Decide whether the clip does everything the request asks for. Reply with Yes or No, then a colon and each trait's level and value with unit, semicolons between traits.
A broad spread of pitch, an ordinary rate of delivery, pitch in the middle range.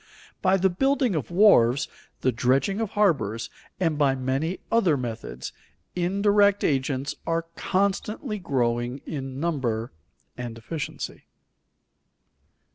No: wide, 7.1 semitones; slow, 110 wpm; medium, 155 Hz